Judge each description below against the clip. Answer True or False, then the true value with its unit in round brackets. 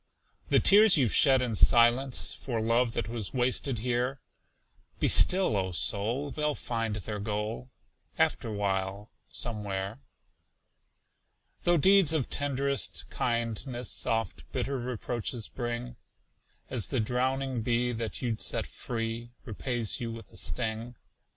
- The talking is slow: True (125 wpm)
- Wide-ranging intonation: False (2.9 semitones)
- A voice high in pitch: False (120 Hz)